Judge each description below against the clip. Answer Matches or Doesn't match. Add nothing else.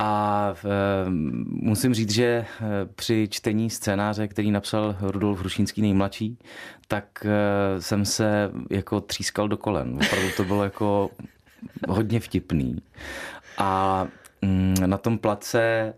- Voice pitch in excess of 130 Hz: Doesn't match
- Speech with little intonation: Matches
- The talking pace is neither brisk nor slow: Doesn't match